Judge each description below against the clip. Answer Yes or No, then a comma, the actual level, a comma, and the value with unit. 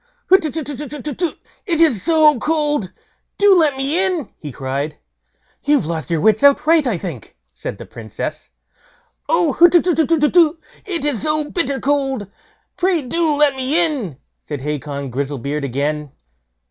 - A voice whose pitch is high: Yes, very high, 280 Hz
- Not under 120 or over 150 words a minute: Yes, slow, 135 wpm